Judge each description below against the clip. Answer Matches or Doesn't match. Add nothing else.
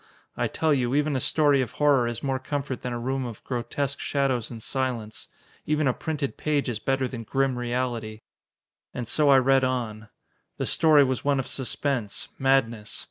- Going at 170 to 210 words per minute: Matches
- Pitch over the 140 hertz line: Doesn't match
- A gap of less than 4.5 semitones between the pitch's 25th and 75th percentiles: Matches